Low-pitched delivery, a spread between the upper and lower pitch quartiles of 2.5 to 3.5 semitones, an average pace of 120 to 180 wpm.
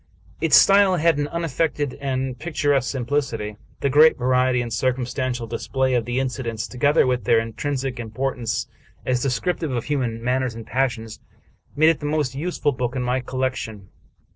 Yes: low, 130 Hz; average, 3.0 semitones; average, 165 wpm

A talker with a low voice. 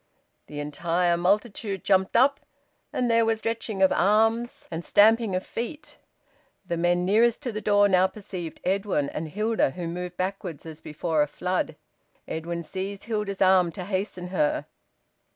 No: high, 190 Hz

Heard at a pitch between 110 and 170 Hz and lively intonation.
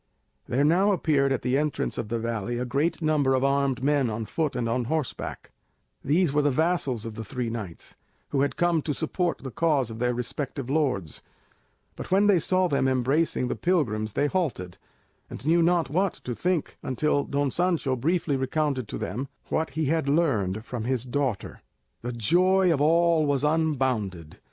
No: medium, 140 Hz; average, 4.7 semitones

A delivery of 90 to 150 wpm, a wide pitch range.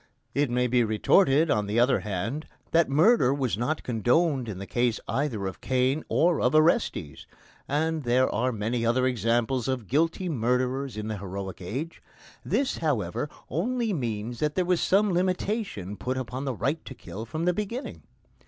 No: average, 170 wpm; wide, 5.9 semitones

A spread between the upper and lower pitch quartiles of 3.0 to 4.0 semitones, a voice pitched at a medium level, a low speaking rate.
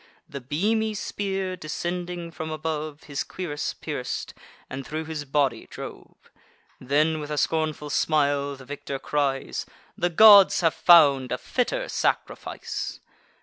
Yes: average, 3.6 semitones; medium, 155 Hz; slow, 130 wpm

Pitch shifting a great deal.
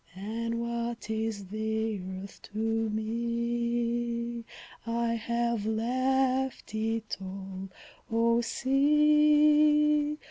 No: narrow, 2.6 semitones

